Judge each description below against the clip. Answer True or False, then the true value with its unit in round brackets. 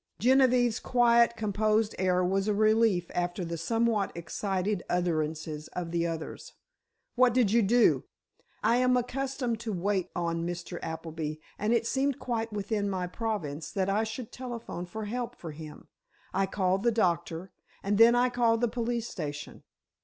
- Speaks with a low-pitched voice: False (210 Hz)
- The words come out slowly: False (155 wpm)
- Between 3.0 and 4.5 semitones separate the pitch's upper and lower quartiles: False (5.0 semitones)